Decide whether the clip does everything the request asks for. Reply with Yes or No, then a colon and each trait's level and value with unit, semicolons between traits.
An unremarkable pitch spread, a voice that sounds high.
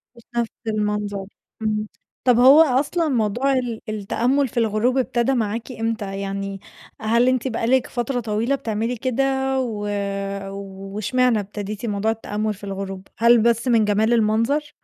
Yes: average, 3.0 semitones; high, 225 Hz